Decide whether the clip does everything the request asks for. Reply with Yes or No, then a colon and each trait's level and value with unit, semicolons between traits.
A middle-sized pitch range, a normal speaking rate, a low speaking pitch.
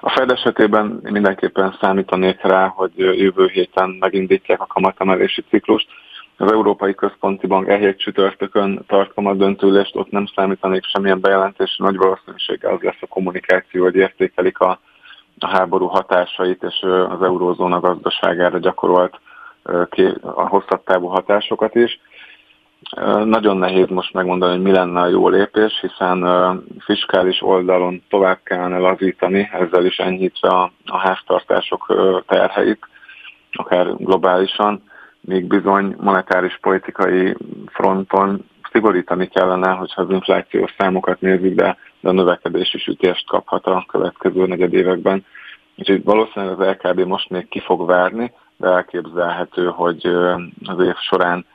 No: narrow, 1.2 semitones; average, 125 wpm; very low, 95 Hz